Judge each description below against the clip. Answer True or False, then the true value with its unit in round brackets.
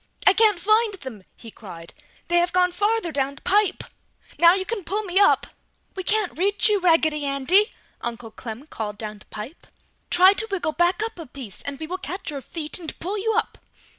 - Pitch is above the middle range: True (345 Hz)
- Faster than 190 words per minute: True (205 wpm)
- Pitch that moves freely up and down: True (6.4 semitones)